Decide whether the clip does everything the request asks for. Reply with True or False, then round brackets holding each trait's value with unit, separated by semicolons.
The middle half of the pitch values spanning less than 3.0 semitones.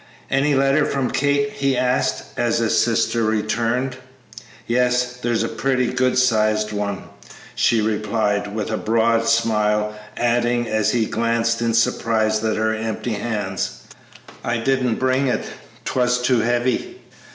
True (2.6 semitones)